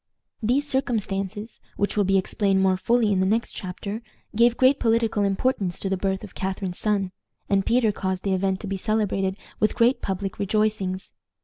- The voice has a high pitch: Yes, high, 200 Hz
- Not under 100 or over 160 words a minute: No, average, 180 wpm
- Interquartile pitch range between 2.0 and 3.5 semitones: Yes, narrow, 2.6 semitones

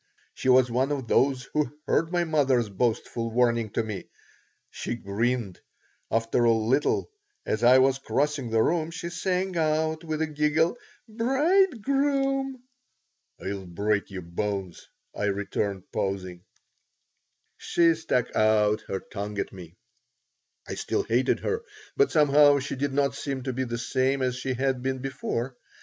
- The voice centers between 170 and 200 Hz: No, low, 130 Hz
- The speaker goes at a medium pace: Yes, average, 150 wpm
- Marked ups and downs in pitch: Yes, wide, 6.0 semitones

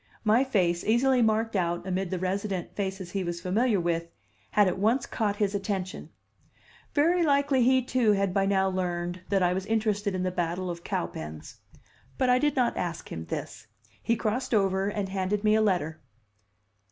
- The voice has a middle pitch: No, high, 195 Hz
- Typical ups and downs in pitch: Yes, average, 3.6 semitones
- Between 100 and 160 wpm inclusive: No, average, 180 wpm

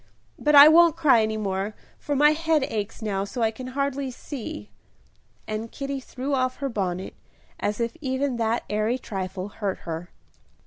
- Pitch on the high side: Yes, high, 235 Hz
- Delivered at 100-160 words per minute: No, average, 170 wpm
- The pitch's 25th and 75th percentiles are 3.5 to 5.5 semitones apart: Yes, average, 5.2 semitones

